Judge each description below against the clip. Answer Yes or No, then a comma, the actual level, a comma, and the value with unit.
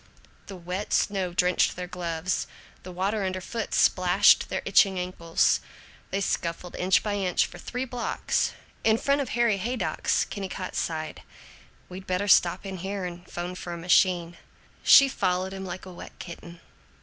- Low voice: No, medium, 185 Hz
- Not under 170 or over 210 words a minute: No, average, 160 wpm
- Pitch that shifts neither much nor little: No, narrow, 2.1 semitones